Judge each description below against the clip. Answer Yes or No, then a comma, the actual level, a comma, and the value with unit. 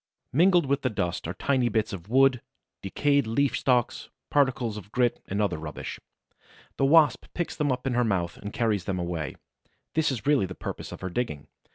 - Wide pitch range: Yes, wide, 6.1 semitones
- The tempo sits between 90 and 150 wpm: No, average, 195 wpm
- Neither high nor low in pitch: No, low, 120 Hz